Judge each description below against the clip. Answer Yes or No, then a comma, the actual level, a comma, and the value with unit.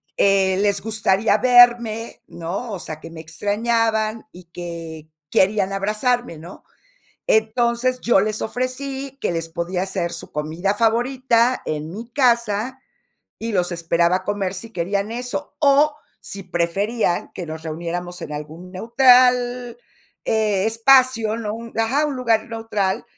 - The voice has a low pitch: No, high, 215 Hz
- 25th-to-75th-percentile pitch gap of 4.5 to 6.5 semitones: Yes, average, 5.1 semitones